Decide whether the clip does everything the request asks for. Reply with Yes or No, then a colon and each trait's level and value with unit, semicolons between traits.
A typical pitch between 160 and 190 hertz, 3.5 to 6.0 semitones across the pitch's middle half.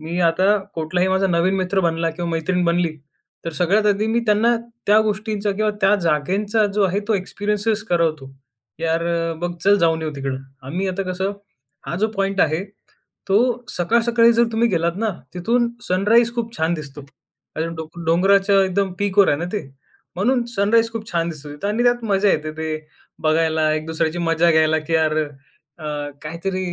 Yes: medium, 185 Hz; average, 4.2 semitones